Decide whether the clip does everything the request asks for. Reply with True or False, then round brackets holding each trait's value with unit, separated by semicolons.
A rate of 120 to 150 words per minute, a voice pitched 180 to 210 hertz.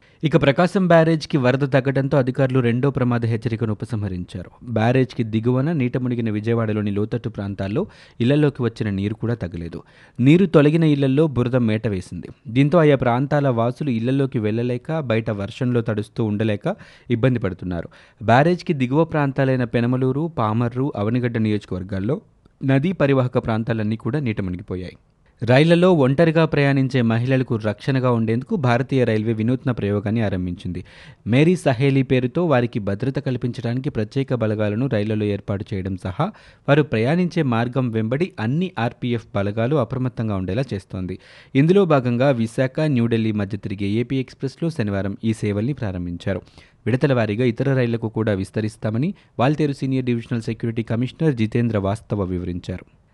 False (125 wpm; 120 Hz)